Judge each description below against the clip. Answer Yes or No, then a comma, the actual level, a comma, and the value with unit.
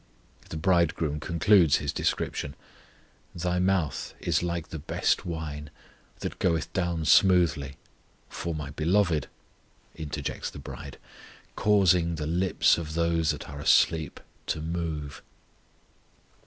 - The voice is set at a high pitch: No, very low, 80 Hz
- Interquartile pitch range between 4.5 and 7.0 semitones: No, narrow, 2.6 semitones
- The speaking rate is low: Yes, slow, 115 wpm